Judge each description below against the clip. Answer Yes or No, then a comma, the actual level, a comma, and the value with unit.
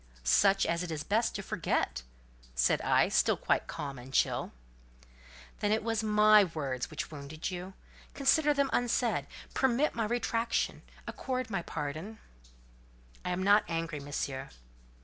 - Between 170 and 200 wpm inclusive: No, average, 145 wpm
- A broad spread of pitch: Yes, wide, 7.3 semitones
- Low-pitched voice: No, high, 190 Hz